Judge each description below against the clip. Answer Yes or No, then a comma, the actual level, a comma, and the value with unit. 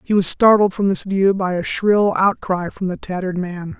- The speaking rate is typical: No, fast, 220 wpm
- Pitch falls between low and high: Yes, medium, 175 Hz